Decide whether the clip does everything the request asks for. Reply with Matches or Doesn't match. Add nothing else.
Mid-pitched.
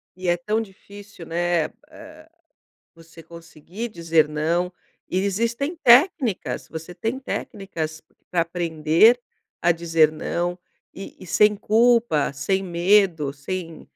Matches